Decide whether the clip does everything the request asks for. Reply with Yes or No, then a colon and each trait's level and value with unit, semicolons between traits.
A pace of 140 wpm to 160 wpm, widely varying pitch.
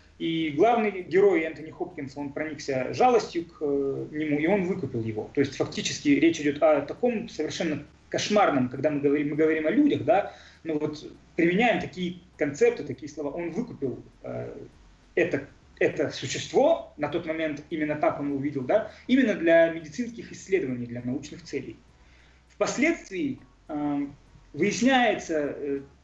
Yes: average, 145 wpm; wide, 6.0 semitones